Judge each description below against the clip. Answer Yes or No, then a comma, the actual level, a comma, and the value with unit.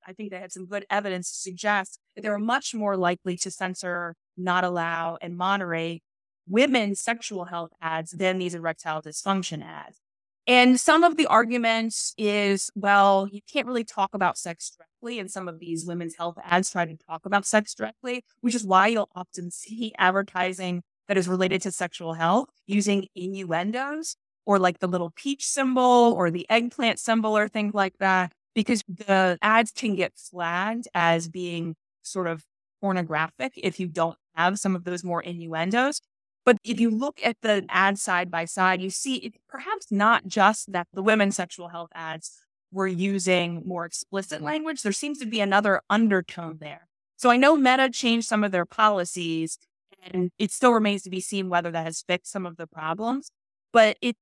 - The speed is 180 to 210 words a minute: Yes, average, 185 wpm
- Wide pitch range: No, average, 3.9 semitones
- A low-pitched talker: No, high, 190 Hz